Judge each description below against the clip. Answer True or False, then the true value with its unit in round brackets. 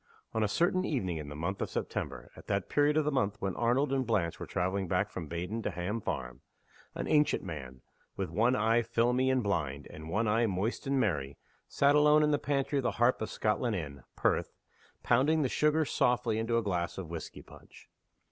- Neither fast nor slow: False (210 wpm)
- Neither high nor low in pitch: False (110 Hz)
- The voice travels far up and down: True (6.7 semitones)